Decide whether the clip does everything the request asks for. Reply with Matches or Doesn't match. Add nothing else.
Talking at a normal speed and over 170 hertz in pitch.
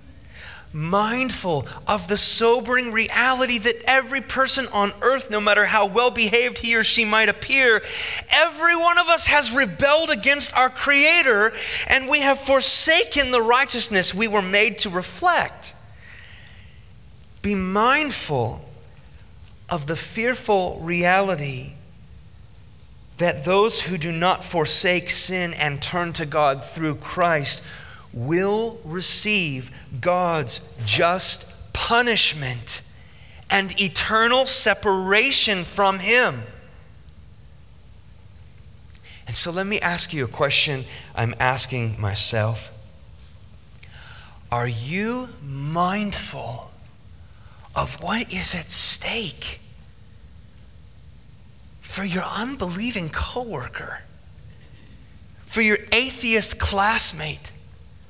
Doesn't match